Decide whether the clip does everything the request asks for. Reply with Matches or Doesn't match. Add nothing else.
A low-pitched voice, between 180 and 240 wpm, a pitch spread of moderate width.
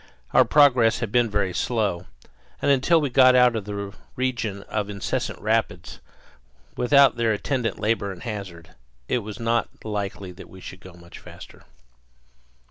Doesn't match